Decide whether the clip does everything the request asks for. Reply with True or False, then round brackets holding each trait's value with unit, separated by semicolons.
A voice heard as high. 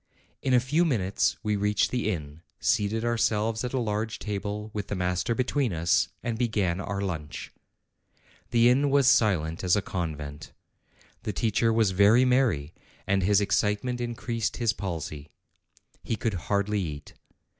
False (105 Hz)